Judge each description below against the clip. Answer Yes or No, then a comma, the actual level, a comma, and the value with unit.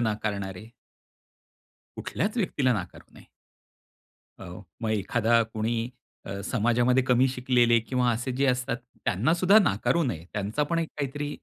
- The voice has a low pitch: Yes, low, 120 Hz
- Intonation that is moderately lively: Yes, average, 4.1 semitones